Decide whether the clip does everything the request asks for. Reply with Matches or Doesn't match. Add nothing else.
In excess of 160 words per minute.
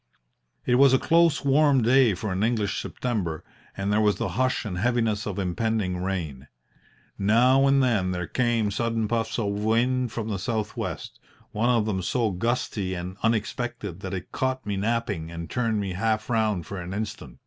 Matches